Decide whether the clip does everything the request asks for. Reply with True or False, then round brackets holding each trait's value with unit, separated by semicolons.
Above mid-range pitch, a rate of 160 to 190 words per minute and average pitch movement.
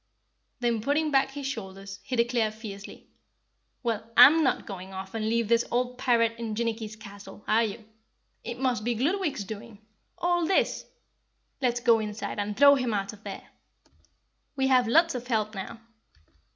True (230 Hz; 165 wpm; 3.1 semitones)